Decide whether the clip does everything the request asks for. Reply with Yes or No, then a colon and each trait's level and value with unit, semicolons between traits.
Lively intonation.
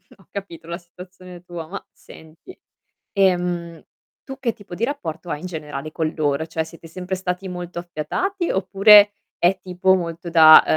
No: average, 2.7 semitones